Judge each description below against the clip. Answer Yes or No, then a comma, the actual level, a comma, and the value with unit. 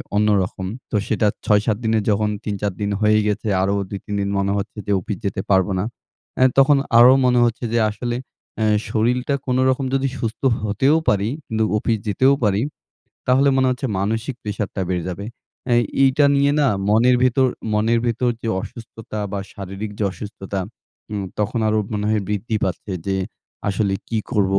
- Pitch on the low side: Yes, low, 110 Hz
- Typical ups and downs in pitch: Yes, average, 3.1 semitones